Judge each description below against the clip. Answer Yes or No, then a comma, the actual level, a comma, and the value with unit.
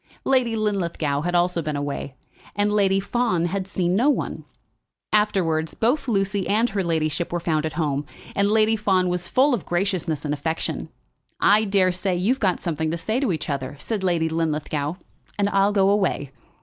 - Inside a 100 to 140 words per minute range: No, average, 175 wpm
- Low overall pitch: No, medium, 185 Hz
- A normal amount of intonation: Yes, average, 4.3 semitones